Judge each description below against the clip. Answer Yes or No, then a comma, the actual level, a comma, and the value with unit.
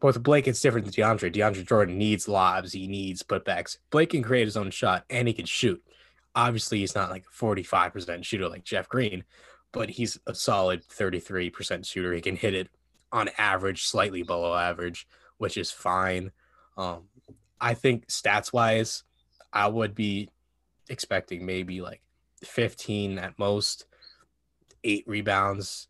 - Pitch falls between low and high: No, low, 100 Hz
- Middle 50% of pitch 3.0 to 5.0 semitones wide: Yes, average, 3.7 semitones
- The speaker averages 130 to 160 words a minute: Yes, average, 155 wpm